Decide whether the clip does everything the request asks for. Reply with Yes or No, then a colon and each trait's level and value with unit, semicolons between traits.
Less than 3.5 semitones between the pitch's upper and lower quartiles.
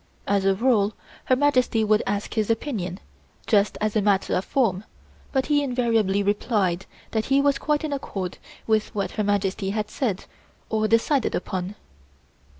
No: average, 4.1 semitones